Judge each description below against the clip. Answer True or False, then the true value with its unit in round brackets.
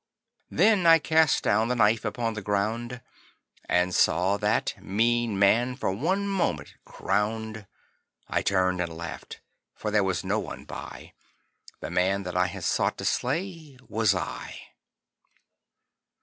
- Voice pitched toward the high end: False (110 Hz)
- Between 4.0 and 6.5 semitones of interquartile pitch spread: True (4.3 semitones)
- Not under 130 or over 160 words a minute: True (140 wpm)